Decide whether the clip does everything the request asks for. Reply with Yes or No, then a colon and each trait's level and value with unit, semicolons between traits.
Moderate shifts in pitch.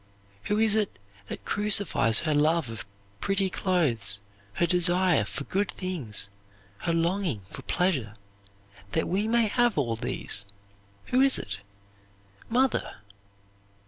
No: wide, 8.7 semitones